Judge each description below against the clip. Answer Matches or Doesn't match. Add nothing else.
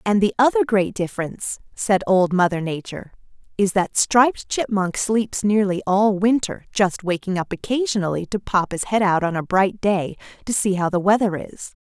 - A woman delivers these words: Matches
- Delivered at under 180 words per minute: Doesn't match